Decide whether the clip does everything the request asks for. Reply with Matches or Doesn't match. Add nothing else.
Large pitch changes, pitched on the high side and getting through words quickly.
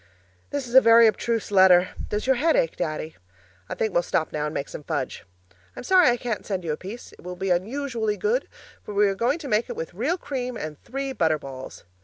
Matches